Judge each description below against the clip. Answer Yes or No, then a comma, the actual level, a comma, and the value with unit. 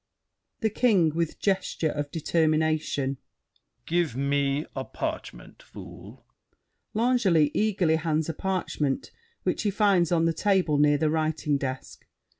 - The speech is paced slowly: Yes, slow, 125 wpm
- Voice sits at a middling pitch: Yes, medium, 160 Hz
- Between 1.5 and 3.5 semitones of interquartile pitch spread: No, average, 4.3 semitones